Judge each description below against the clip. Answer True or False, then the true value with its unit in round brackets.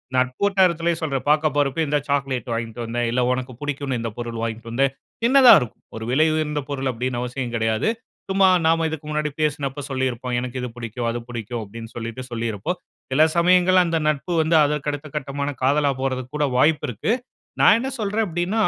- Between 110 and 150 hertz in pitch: True (135 Hz)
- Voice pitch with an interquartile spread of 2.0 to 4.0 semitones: False (4.5 semitones)